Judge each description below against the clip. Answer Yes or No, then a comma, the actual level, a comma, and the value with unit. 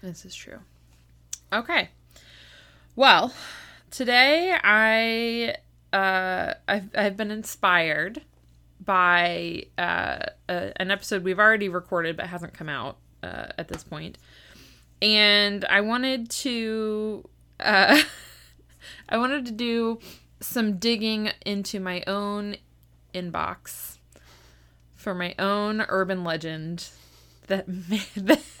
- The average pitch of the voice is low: No, high, 195 Hz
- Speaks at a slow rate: Yes, slow, 110 wpm